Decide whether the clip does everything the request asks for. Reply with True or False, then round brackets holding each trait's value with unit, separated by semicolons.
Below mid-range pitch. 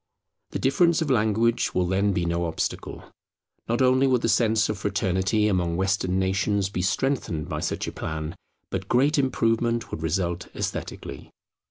True (100 Hz)